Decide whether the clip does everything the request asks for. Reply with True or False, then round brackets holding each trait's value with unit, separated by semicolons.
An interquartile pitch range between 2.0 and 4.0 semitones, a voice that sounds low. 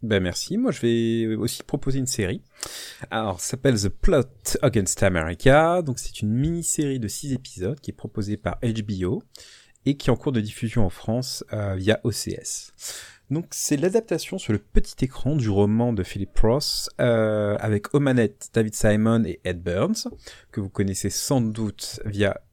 False (4.5 semitones; 115 Hz)